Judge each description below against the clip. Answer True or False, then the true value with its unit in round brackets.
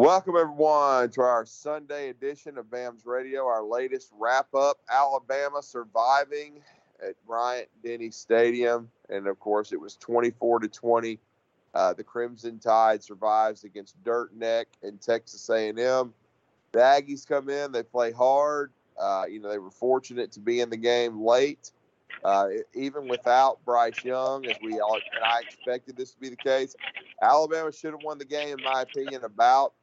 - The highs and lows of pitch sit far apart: False (3.6 semitones)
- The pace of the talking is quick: False (165 wpm)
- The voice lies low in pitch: True (125 Hz)